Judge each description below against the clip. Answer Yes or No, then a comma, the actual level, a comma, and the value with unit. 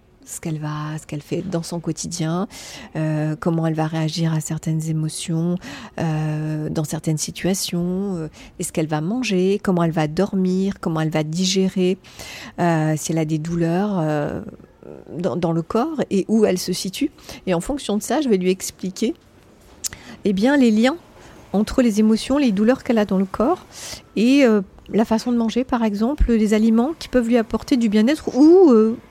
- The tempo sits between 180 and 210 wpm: Yes, average, 190 wpm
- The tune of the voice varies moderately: No, wide, 5.7 semitones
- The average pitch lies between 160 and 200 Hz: Yes, medium, 185 Hz